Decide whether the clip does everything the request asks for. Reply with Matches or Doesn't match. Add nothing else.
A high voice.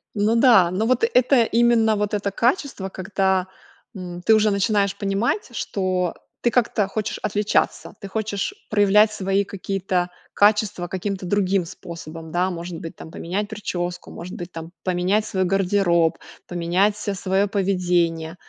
Matches